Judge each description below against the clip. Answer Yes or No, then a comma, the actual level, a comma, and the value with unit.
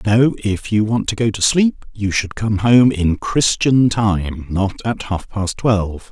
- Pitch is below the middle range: Yes, low, 105 Hz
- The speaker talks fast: No, average, 195 wpm